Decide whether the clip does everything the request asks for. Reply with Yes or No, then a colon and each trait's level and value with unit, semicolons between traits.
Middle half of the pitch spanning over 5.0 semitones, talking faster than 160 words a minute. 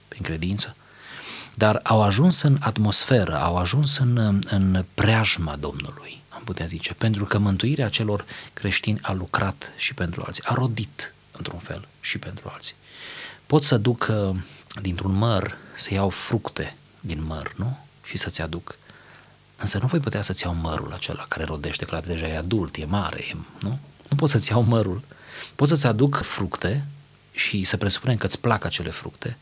Yes: wide, 5.4 semitones; fast, 170 wpm